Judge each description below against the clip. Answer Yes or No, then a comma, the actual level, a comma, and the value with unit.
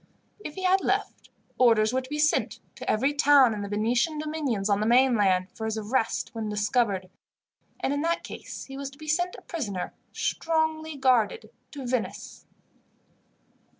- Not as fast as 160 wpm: No, average, 170 wpm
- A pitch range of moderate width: No, wide, 5.8 semitones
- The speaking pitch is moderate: No, very high, 255 Hz